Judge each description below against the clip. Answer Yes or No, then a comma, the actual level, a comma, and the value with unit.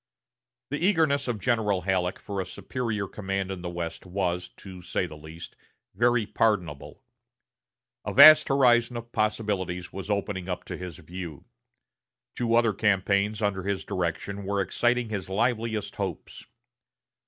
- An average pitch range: Yes, average, 3.9 semitones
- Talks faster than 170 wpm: No, average, 140 wpm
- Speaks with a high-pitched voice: No, low, 100 Hz